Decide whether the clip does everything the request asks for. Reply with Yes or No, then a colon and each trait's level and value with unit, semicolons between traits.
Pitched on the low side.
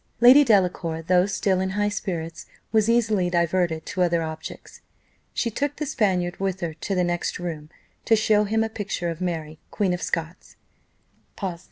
No: medium, 185 Hz